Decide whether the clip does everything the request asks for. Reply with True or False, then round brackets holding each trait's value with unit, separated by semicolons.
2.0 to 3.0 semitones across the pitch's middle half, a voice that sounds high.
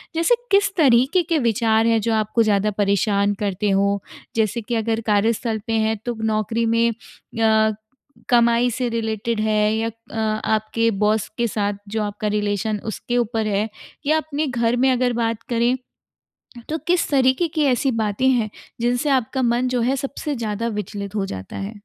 True (2.5 semitones; 225 Hz)